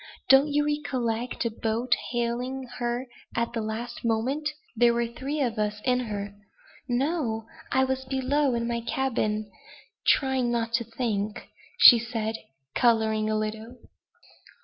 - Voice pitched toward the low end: No, high, 235 Hz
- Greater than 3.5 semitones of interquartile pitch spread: No, average, 2.8 semitones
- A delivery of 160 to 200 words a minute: No, average, 140 wpm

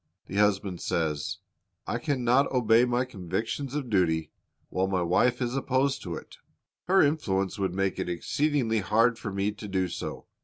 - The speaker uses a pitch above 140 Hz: No, low, 105 Hz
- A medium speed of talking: Yes, average, 170 wpm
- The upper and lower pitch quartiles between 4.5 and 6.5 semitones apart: Yes, average, 5.1 semitones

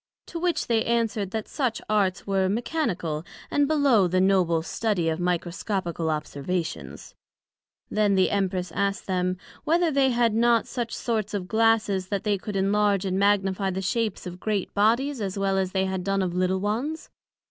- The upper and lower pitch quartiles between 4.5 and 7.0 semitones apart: No, average, 3.5 semitones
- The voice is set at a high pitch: Yes, high, 195 Hz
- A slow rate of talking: No, average, 170 wpm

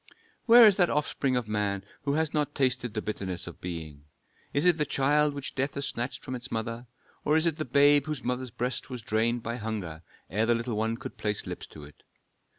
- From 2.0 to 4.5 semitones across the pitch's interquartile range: No, average, 5.1 semitones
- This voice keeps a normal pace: No, fast, 220 wpm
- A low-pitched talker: Yes, low, 125 Hz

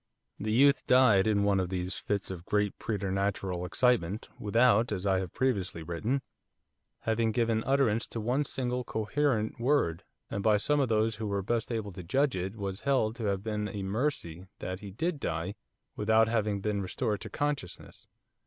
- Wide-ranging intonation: No, average, 3.8 semitones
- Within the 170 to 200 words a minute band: Yes, average, 180 wpm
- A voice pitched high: No, low, 105 Hz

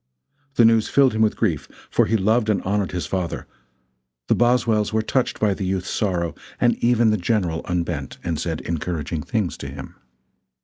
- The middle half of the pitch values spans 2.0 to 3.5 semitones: No, average, 4.5 semitones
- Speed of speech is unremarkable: Yes, average, 180 wpm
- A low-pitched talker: Yes, low, 100 Hz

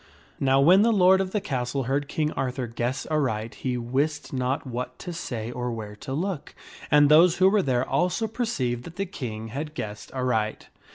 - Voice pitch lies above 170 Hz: No, low, 135 Hz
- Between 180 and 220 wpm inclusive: Yes, average, 195 wpm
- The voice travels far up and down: Yes, wide, 5.9 semitones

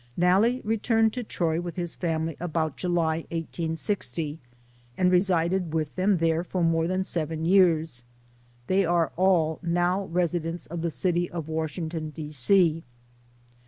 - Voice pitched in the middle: Yes, medium, 170 Hz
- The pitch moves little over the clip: Yes, narrow, 2.3 semitones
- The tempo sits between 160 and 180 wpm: No, average, 140 wpm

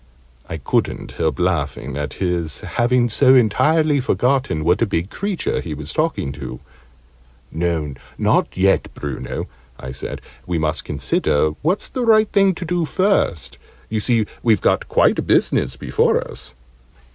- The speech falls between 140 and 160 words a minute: Yes, average, 150 wpm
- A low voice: Yes, very low, 95 Hz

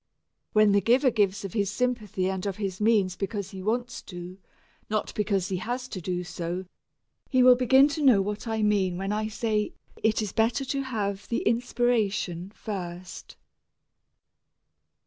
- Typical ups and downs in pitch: Yes, average, 3.6 semitones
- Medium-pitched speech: No, high, 210 Hz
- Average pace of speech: Yes, average, 165 wpm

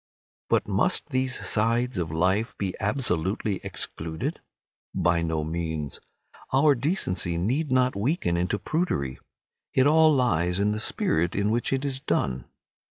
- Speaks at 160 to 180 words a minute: No, average, 140 wpm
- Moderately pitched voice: No, low, 100 Hz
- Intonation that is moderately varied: No, wide, 7.2 semitones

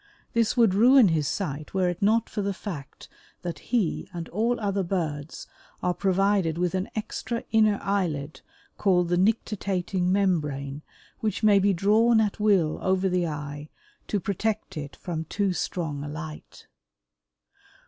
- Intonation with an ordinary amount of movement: Yes, average, 4.2 semitones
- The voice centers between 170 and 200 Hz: Yes, medium, 185 Hz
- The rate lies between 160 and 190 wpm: No, average, 150 wpm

